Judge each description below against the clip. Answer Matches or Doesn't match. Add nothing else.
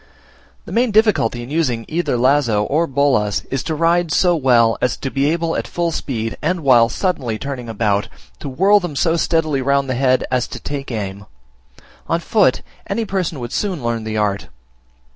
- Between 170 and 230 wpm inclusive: Matches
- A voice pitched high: Doesn't match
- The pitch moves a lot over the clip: Matches